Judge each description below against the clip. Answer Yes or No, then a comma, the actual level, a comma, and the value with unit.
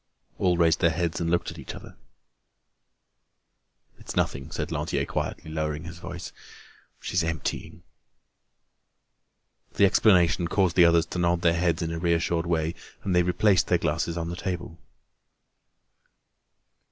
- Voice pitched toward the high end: No, very low, 85 Hz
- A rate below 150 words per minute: Yes, average, 140 wpm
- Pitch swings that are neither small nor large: No, narrow, 1.2 semitones